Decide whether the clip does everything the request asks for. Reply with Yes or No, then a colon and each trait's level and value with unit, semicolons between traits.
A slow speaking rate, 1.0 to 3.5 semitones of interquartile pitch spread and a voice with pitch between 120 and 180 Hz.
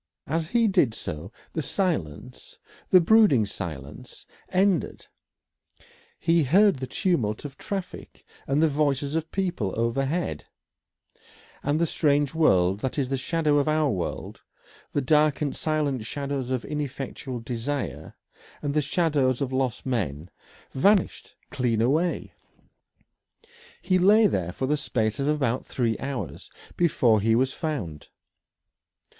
No: slow, 130 wpm; average, 5.3 semitones; medium, 140 Hz